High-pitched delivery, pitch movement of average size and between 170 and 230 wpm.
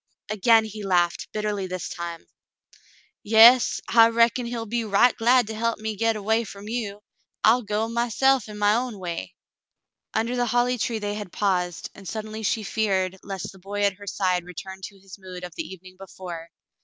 Yes: high, 210 Hz; average, 3.2 semitones; average, 195 wpm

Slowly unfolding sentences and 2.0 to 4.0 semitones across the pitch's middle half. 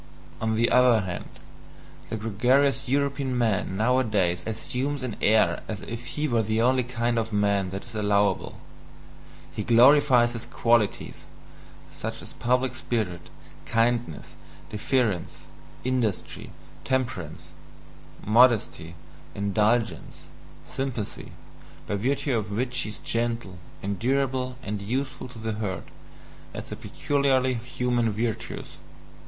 Yes: slow, 115 wpm; average, 3.4 semitones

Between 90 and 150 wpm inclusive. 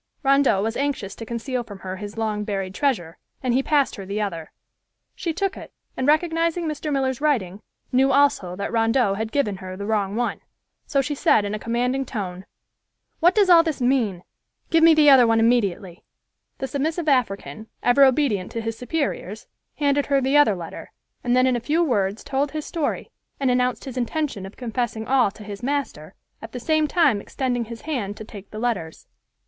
No: average, 195 wpm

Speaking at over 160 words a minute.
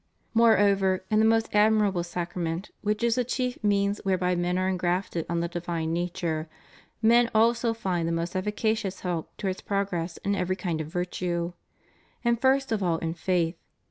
Yes: average, 175 wpm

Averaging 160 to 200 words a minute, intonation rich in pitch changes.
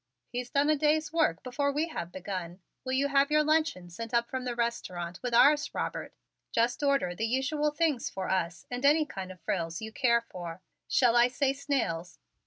Yes: average, 195 wpm; wide, 7.2 semitones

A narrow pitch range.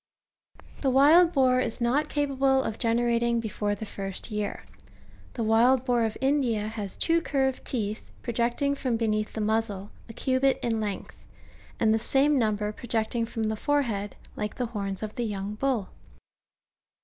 No: average, 3.6 semitones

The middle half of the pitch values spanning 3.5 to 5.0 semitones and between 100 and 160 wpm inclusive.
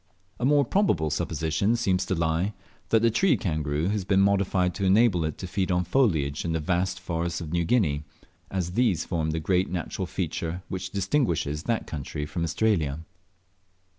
No: average, 3.8 semitones; average, 175 wpm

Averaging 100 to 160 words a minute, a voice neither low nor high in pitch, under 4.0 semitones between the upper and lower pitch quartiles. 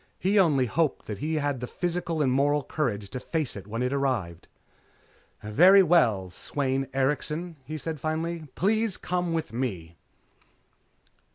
No: average, 150 wpm; medium, 145 Hz; average, 5.0 semitones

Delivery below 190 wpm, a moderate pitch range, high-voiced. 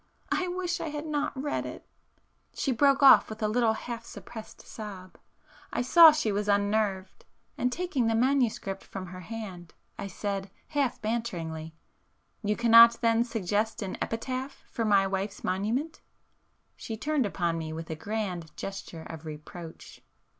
Yes: average, 150 wpm; average, 4.6 semitones; high, 220 Hz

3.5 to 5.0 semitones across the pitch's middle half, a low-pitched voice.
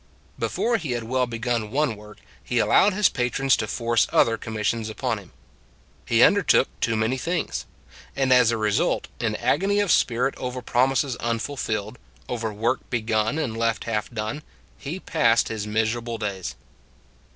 No: average, 3.0 semitones; low, 115 Hz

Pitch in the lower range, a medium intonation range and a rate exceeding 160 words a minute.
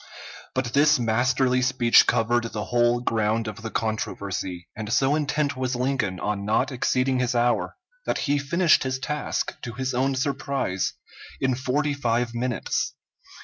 No: low, 125 Hz; average, 3.0 semitones; average, 150 wpm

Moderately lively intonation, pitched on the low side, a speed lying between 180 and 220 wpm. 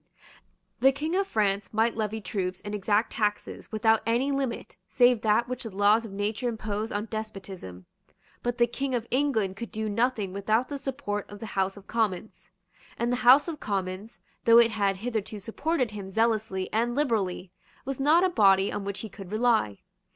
No: average, 3.2 semitones; high, 220 Hz; average, 185 wpm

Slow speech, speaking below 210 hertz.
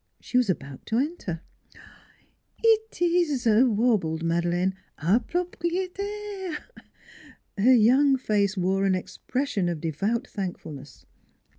No: slow, 125 wpm; high, 225 Hz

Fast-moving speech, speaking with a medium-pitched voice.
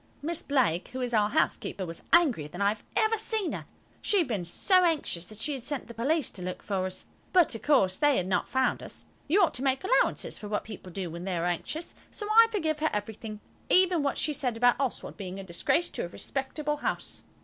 No: fast, 235 wpm; very high, 250 Hz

